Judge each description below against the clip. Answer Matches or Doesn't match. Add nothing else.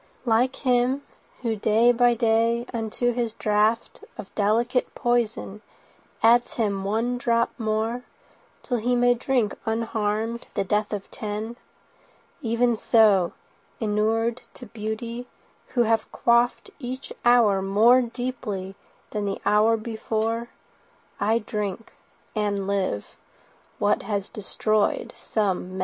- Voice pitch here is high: Matches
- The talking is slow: Matches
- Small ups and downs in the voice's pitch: Matches